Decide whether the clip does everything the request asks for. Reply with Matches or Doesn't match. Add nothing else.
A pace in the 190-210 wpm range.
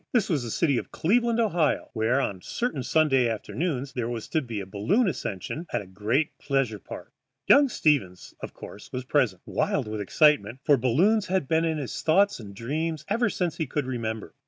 Matches